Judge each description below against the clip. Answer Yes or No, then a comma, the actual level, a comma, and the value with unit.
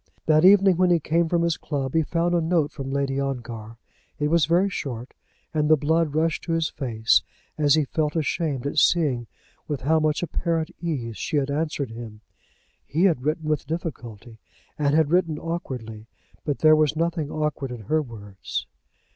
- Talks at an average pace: Yes, average, 180 wpm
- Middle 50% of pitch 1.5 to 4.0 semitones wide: Yes, average, 3.6 semitones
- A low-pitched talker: No, medium, 150 Hz